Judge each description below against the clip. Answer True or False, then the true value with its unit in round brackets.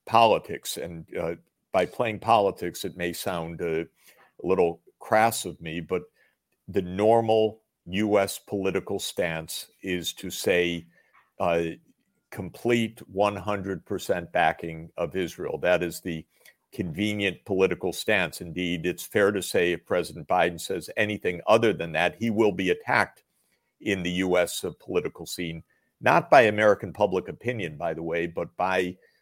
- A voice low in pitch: True (90 Hz)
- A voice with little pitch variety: False (3.2 semitones)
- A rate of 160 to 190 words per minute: False (140 wpm)